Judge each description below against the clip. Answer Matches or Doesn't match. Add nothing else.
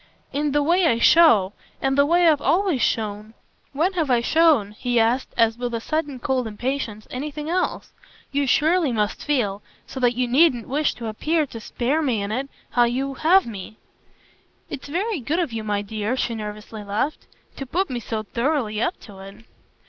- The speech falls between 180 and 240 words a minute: Matches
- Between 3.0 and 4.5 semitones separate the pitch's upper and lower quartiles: Doesn't match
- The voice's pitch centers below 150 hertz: Doesn't match